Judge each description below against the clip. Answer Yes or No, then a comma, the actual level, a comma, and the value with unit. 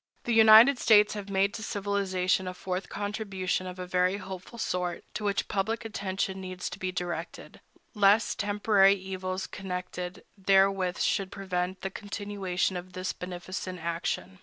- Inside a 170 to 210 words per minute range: No, average, 150 wpm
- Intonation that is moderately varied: No, narrow, 1.8 semitones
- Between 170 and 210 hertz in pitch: Yes, high, 190 Hz